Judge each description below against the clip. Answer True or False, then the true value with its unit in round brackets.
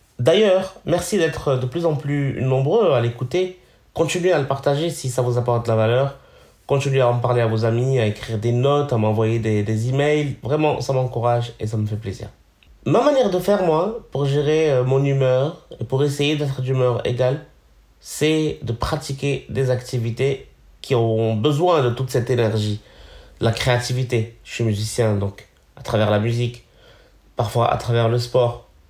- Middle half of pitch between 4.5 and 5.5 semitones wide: False (3.7 semitones)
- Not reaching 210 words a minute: True (180 wpm)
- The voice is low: True (125 Hz)